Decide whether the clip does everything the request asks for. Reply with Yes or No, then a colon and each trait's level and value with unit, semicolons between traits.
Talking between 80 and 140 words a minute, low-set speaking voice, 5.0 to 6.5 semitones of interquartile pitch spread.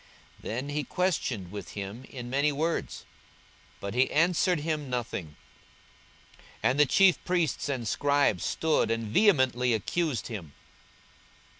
Yes: slow, 135 wpm; low, 130 Hz; wide, 5.4 semitones